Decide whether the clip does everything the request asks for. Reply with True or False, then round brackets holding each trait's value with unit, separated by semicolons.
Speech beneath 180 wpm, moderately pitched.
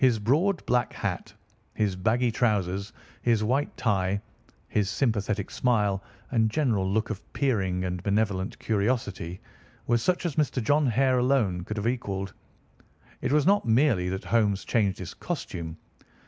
False (145 wpm; 110 Hz)